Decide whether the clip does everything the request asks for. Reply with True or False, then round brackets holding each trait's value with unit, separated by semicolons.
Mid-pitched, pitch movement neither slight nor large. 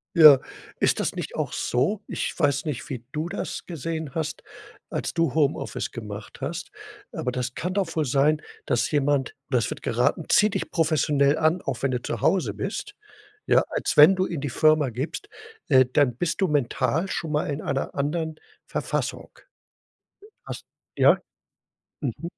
True (150 Hz; 3.7 semitones)